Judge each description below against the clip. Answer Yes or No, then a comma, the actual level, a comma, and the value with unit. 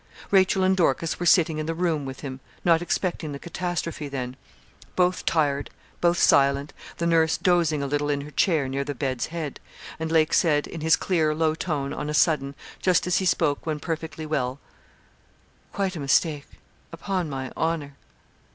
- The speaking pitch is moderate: Yes, medium, 160 Hz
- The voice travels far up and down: No, average, 3.2 semitones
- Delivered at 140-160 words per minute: No, average, 180 wpm